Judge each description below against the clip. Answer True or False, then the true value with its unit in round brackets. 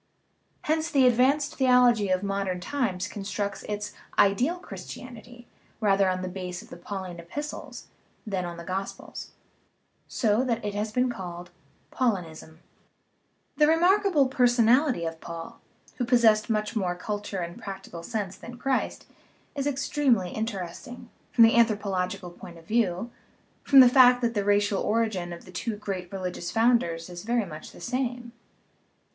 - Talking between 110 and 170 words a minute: True (150 wpm)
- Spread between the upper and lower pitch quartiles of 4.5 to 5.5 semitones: True (5.1 semitones)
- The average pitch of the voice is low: False (210 Hz)